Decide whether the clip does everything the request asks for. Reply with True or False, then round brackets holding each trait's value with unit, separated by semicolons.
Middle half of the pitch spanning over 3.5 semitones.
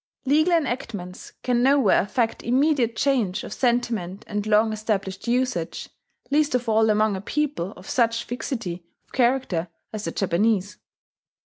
True (4.0 semitones)